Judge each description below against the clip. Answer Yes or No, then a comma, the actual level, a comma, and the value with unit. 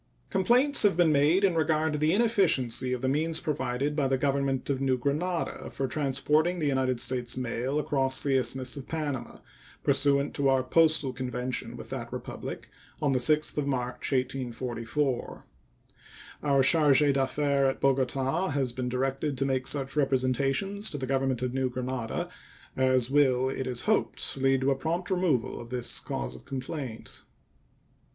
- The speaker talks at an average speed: Yes, average, 165 wpm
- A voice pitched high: No, low, 135 Hz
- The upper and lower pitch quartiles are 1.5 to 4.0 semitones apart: Yes, narrow, 2.6 semitones